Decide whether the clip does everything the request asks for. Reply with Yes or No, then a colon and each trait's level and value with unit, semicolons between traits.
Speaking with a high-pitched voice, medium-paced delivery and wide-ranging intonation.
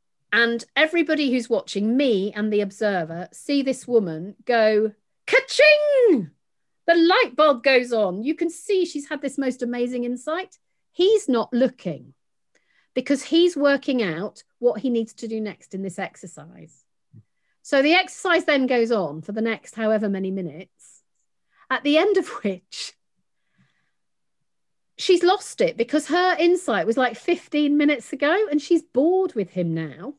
Yes: very high, 255 Hz; average, 155 wpm; wide, 6.6 semitones